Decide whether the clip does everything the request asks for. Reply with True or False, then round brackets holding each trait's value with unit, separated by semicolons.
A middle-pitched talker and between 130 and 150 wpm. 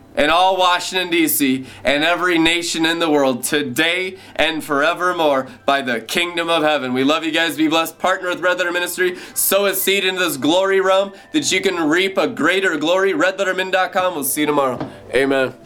False (175 Hz; 190 wpm)